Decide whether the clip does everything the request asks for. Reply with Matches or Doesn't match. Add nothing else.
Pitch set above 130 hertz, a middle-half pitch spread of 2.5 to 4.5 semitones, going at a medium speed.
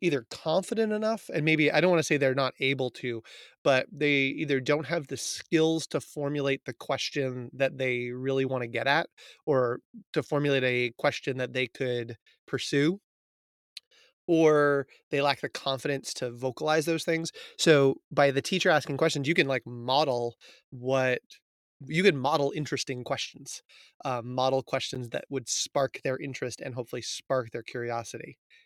Matches